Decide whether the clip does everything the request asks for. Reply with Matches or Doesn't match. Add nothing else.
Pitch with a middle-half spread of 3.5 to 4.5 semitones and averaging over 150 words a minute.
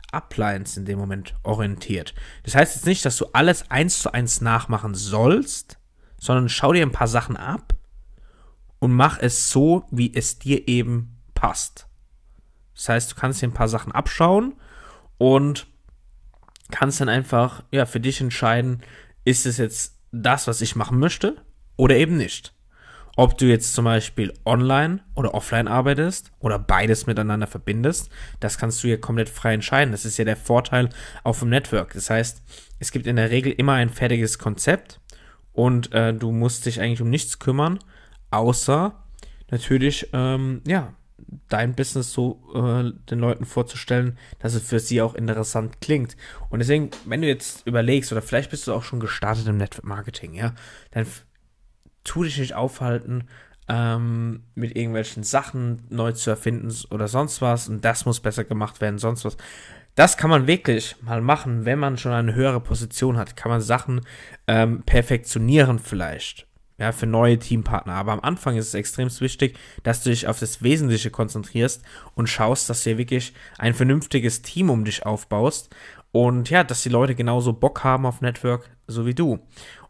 Doesn't match